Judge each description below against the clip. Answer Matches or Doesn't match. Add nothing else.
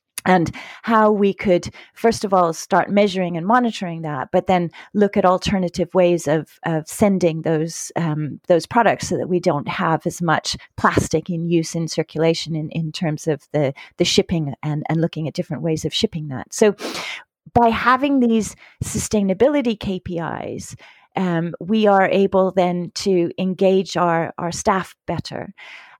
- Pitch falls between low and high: Matches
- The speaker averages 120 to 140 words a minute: Doesn't match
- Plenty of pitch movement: Doesn't match